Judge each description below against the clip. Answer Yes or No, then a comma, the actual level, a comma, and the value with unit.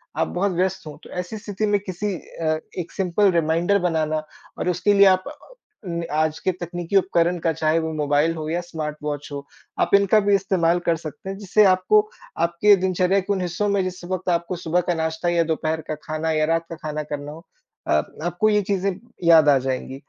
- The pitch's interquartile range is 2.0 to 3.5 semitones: Yes, average, 3.0 semitones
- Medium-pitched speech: Yes, medium, 175 Hz